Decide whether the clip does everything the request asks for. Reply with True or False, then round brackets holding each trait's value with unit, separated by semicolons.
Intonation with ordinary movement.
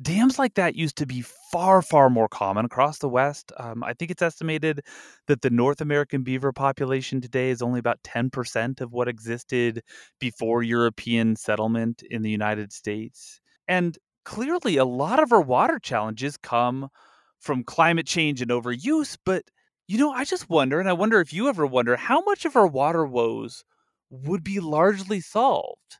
False (6.8 semitones)